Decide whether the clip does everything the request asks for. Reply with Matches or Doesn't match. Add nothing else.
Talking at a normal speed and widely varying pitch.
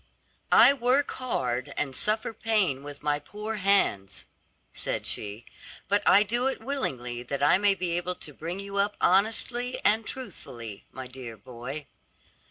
Matches